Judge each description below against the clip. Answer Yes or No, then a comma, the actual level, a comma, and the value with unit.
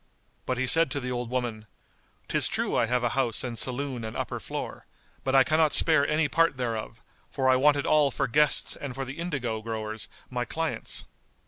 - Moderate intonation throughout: Yes, average, 3.2 semitones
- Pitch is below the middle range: Yes, low, 130 Hz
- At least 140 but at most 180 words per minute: No, fast, 205 wpm